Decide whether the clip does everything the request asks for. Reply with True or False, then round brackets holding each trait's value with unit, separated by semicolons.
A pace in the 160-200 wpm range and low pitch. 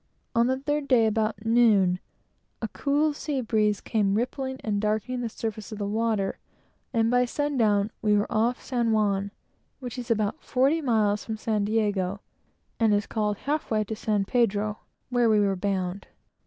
False (175 wpm; 220 Hz)